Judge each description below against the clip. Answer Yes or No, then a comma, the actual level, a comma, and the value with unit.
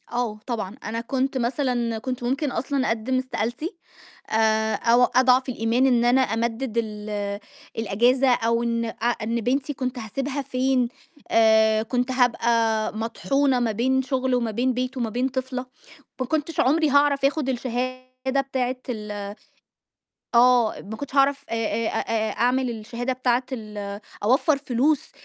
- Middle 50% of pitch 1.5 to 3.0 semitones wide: Yes, narrow, 2.6 semitones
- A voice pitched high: Yes, high, 245 Hz